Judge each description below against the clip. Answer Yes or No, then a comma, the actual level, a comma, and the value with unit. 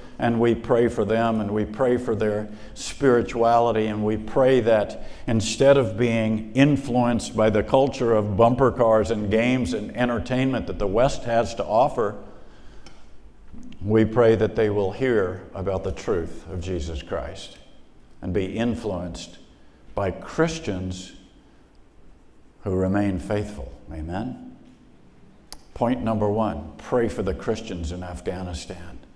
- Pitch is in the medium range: No, low, 110 Hz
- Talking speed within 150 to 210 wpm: No, slow, 135 wpm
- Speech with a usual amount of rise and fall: Yes, average, 4.1 semitones